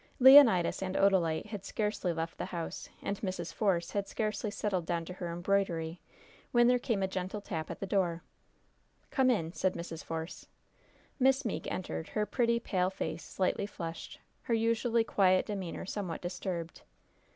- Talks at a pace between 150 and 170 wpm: Yes, average, 160 wpm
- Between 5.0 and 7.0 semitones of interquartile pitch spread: No, average, 3.8 semitones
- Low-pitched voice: No, high, 190 Hz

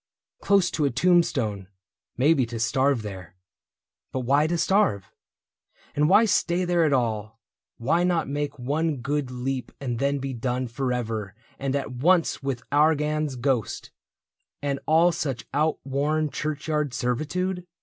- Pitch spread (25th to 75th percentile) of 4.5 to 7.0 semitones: No, average, 4.1 semitones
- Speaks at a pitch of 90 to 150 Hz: Yes, medium, 140 Hz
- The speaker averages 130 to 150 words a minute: Yes, average, 140 wpm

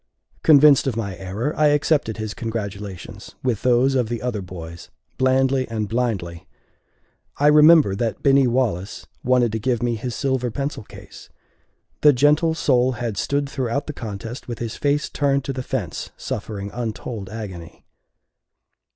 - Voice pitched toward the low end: Yes, low, 120 Hz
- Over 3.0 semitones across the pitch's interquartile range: Yes, average, 4.3 semitones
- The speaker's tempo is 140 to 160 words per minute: Yes, average, 150 wpm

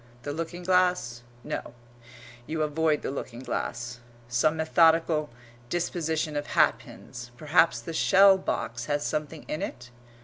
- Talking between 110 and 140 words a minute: Yes, slow, 135 wpm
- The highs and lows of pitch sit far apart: No, average, 4.2 semitones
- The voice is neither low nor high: Yes, medium, 155 Hz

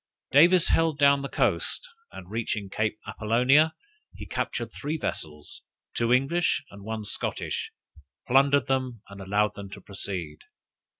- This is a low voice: Yes, low, 115 Hz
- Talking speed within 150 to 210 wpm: No, slow, 135 wpm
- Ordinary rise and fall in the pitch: No, wide, 5.8 semitones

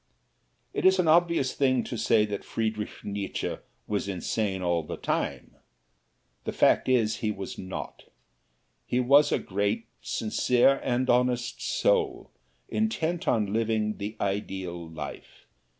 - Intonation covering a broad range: No, average, 4.6 semitones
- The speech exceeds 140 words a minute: No, slow, 135 wpm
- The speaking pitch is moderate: No, low, 110 Hz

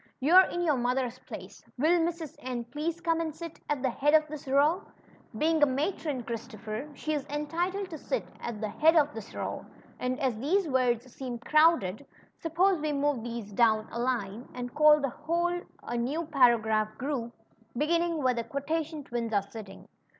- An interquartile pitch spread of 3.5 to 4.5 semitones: No, average, 5.0 semitones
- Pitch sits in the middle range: No, very high, 280 Hz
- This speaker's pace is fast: No, average, 165 wpm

